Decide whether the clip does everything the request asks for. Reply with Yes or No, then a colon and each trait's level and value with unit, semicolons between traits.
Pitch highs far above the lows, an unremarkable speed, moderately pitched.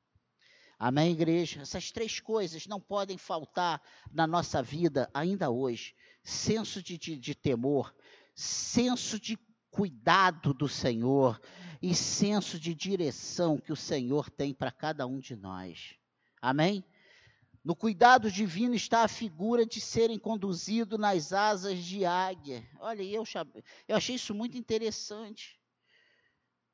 Yes: wide, 7.2 semitones; average, 130 wpm; medium, 180 Hz